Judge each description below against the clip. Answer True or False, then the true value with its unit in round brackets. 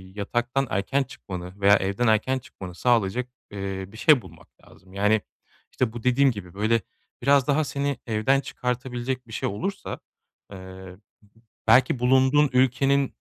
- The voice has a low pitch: True (120 Hz)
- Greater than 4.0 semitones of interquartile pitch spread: True (4.9 semitones)